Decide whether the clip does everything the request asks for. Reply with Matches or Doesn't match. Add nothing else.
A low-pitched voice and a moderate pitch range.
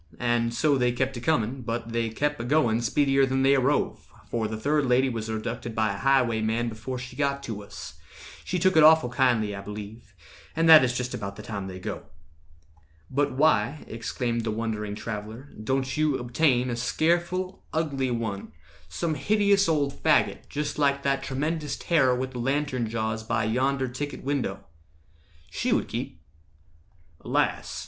Matches